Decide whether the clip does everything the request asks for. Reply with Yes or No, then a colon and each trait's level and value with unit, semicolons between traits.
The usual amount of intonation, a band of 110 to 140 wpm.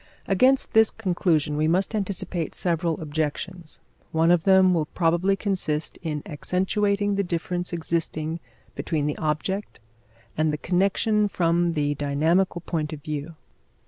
Yes: average, 3.5 semitones; slow, 135 wpm